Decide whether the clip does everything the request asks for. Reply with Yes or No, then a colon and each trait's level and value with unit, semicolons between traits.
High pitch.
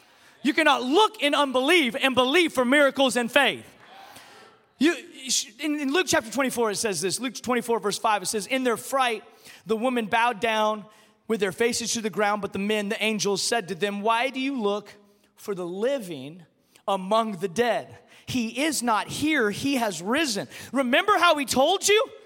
Yes: high, 235 Hz